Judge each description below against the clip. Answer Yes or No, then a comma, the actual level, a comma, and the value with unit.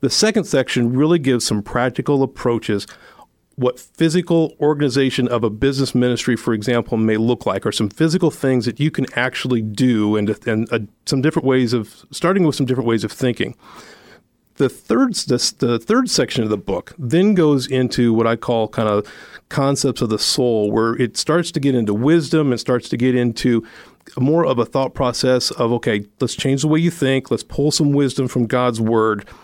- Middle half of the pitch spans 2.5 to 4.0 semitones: Yes, average, 3.6 semitones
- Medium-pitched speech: No, low, 125 Hz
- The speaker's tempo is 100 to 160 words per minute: No, average, 195 wpm